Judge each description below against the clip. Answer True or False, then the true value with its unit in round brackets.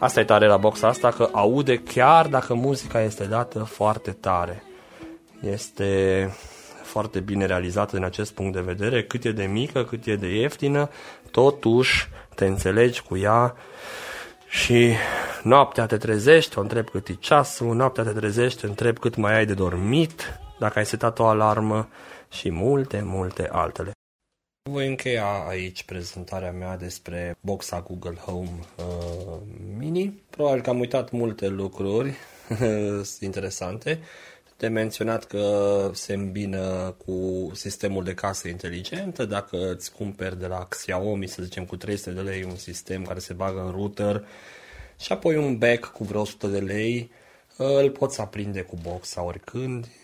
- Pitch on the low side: True (105 Hz)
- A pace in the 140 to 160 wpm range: True (150 wpm)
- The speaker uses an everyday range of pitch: True (4.2 semitones)